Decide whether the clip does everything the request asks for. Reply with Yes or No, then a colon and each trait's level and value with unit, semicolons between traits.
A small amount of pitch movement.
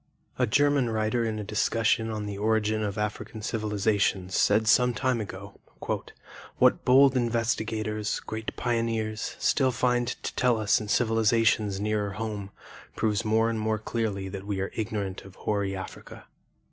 Yes: narrow, 1.7 semitones